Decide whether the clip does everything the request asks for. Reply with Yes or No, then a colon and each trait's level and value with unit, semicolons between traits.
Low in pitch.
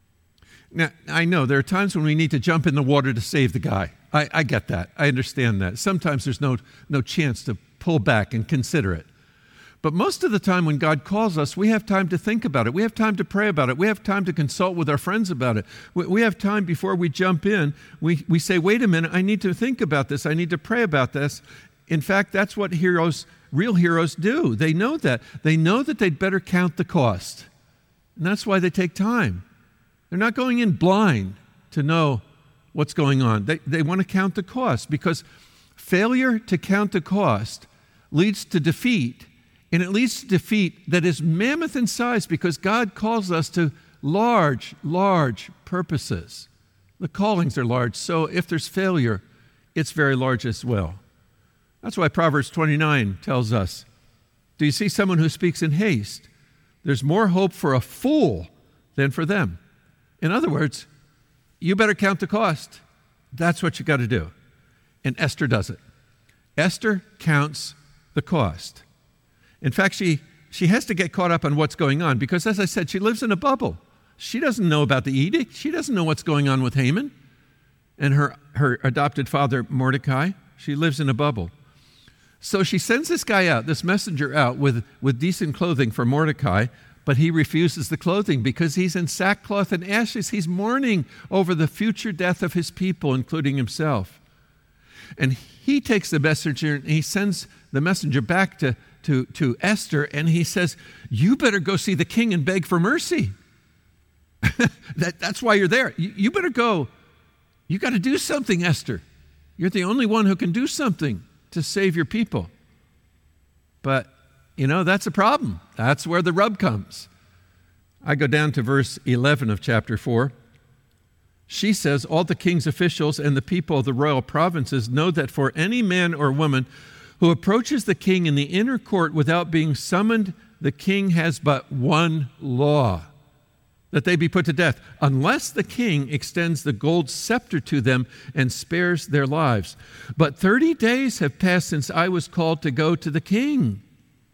No: medium, 160 Hz